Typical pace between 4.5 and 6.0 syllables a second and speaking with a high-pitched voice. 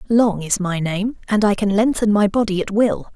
Yes: 5.0 syllables/s; high, 205 Hz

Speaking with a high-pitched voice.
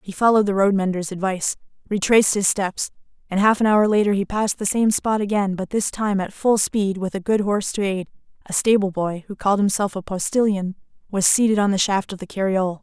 Yes: high, 200 Hz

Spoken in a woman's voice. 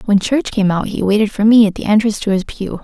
Yes: female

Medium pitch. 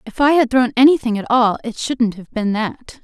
No: high, 240 Hz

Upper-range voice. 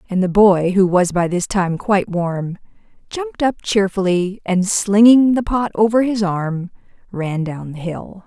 Yes: high, 195 Hz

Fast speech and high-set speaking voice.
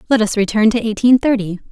Yes: fast, 210 wpm; high, 220 Hz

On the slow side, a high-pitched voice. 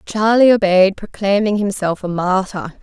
Yes: slow, 130 wpm; high, 195 Hz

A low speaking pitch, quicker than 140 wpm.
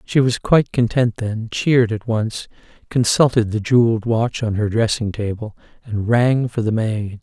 Yes: low, 115 Hz; average, 175 wpm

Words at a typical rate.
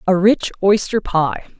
Yes: average, 150 wpm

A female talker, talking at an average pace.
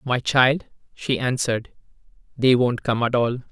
No: male; average, 155 wpm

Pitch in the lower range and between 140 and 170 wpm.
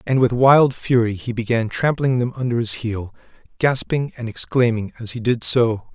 No: low, 120 Hz; average, 180 wpm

